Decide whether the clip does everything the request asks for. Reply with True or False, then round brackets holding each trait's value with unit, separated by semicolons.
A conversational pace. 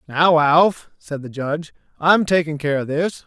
True (185 wpm)